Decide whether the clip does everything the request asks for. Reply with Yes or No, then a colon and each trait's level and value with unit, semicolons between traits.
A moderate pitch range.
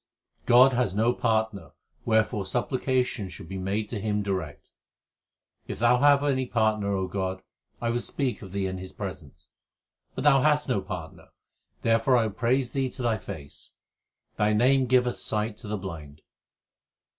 Yes: average, 4.4 semitones